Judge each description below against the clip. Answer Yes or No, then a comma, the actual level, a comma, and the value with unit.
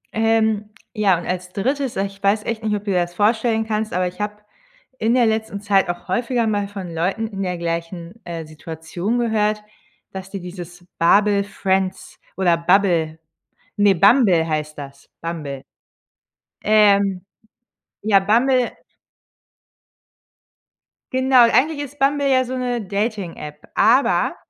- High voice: Yes, high, 200 Hz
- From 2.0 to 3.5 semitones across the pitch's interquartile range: No, average, 4.0 semitones